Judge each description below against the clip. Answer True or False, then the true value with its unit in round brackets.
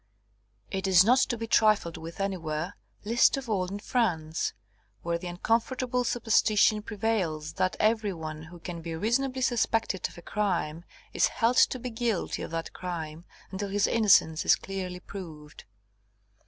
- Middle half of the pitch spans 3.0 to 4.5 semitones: False (5.0 semitones)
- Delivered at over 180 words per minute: False (155 wpm)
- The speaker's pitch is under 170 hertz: False (195 Hz)